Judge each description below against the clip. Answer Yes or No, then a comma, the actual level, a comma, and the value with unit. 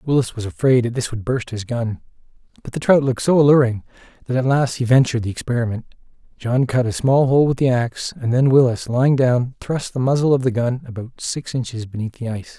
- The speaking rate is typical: No, fast, 225 wpm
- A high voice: No, low, 125 Hz